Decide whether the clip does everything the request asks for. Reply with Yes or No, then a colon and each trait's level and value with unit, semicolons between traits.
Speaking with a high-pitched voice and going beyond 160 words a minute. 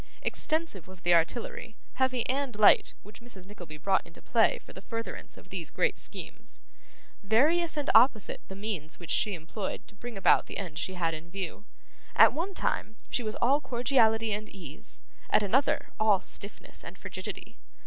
Yes: high, 215 Hz; average, 175 wpm